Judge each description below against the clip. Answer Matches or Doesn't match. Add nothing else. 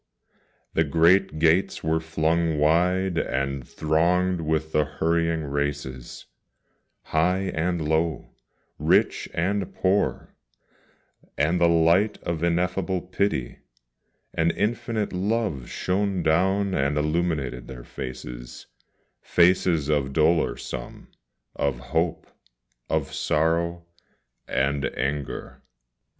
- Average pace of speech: Doesn't match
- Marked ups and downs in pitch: Doesn't match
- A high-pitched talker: Doesn't match